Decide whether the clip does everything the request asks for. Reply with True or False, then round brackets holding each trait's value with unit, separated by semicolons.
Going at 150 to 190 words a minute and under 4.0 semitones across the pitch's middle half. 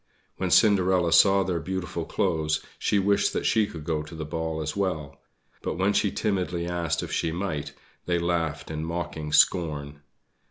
True (170 wpm; 3.1 semitones)